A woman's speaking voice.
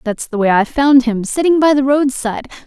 Yes: female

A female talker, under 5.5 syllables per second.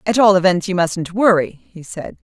Yes: female; 4.8 syllables/s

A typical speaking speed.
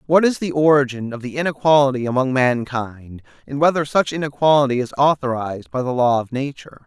Yes: average, 175 wpm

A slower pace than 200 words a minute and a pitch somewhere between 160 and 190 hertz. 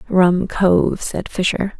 Yes: slow, 135 wpm; medium, 185 Hz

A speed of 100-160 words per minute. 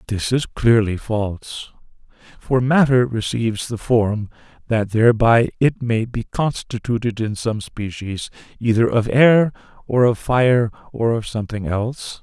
Yes: average, 140 wpm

